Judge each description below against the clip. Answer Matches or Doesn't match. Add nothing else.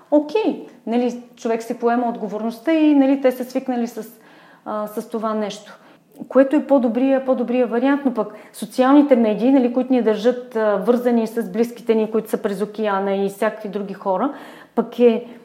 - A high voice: Matches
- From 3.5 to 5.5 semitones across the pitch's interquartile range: Doesn't match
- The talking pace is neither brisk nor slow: Doesn't match